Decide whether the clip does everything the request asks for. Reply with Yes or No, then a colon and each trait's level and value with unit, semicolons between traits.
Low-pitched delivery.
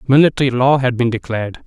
Yes: low, 125 Hz